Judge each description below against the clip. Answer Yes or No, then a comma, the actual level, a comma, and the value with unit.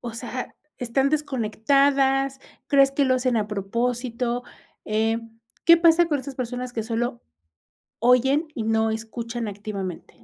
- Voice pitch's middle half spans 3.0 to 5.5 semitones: Yes, average, 3.4 semitones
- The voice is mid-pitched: No, high, 245 Hz